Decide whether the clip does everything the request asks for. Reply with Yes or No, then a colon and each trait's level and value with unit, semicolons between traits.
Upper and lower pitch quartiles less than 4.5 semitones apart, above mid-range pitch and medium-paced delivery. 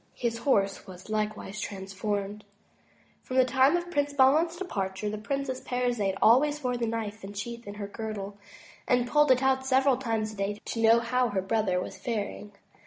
Yes: average, 4.1 semitones; high, 230 Hz; average, 180 wpm